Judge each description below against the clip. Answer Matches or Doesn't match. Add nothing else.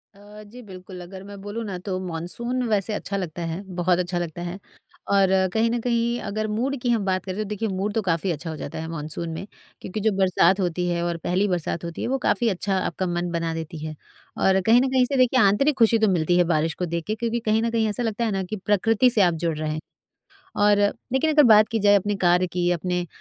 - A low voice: Doesn't match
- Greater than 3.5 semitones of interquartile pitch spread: Matches